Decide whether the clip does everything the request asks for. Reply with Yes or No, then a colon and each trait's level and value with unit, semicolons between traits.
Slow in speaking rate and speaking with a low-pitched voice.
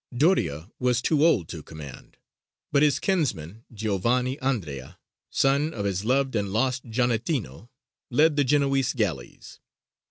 Yes: slow, 130 wpm; low, 125 Hz